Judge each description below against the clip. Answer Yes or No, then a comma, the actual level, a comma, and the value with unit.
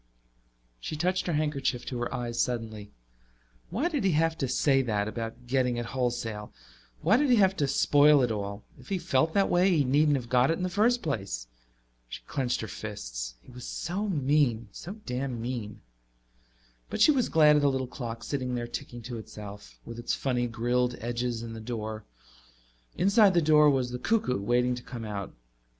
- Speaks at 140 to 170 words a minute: No, average, 195 wpm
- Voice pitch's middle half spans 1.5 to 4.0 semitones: No, average, 4.8 semitones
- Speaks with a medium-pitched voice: No, low, 125 Hz